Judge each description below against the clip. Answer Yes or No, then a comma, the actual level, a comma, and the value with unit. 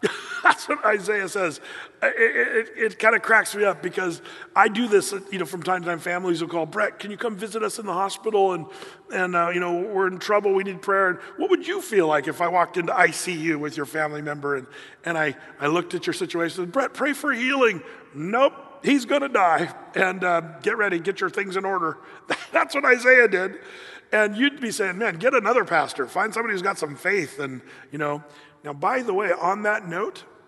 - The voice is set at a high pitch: Yes, high, 195 Hz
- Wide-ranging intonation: Yes, wide, 7.4 semitones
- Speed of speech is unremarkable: No, fast, 225 wpm